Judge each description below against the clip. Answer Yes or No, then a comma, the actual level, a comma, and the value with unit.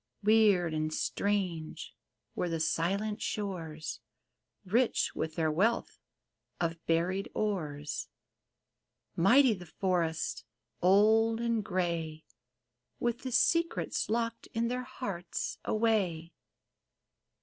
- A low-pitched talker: No, high, 190 Hz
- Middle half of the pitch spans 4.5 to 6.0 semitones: Yes, average, 5.2 semitones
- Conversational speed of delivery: No, slow, 95 wpm